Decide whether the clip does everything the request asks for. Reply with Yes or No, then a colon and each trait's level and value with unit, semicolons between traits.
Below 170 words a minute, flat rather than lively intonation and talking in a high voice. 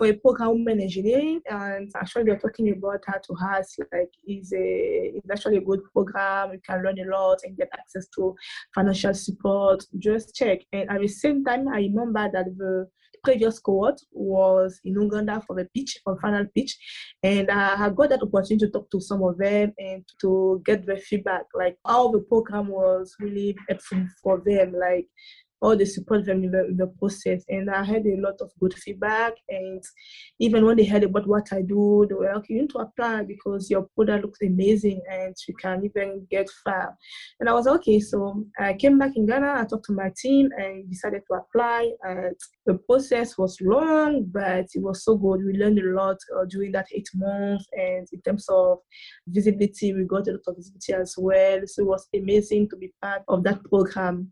No: fast, 205 wpm; narrow, 2.3 semitones; high, 200 Hz